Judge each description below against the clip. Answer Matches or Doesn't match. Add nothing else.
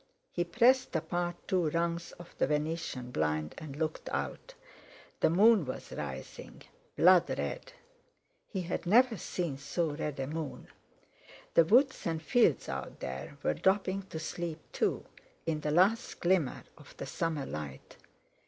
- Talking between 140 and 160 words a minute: Matches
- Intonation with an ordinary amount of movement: Matches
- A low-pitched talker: Doesn't match